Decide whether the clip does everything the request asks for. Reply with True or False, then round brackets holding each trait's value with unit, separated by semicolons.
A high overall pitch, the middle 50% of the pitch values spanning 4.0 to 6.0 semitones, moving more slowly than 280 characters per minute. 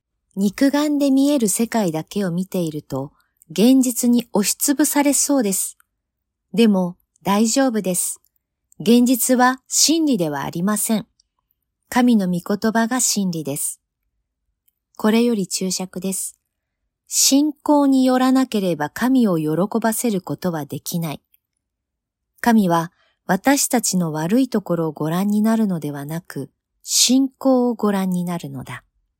False (200 Hz; 7.2 semitones; 245 characters per minute)